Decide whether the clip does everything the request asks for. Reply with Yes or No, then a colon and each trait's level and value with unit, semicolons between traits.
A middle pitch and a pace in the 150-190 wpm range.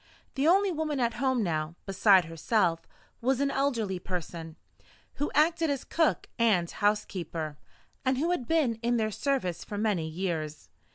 No: high, 220 Hz; average, 155 wpm